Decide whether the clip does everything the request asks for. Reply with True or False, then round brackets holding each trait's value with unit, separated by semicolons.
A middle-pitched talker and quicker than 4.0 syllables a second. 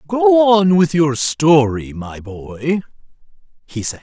False (145 Hz; 3.3 syllables/s)